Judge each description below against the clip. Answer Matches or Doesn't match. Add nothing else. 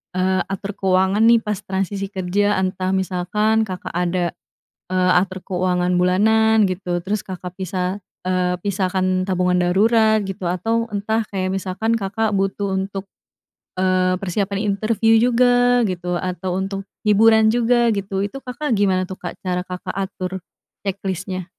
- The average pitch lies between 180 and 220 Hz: Matches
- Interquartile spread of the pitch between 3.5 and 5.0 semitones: Doesn't match